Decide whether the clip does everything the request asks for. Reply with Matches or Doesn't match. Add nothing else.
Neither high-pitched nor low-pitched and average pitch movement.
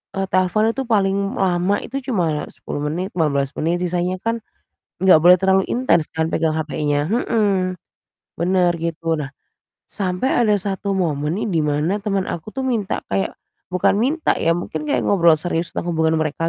Matches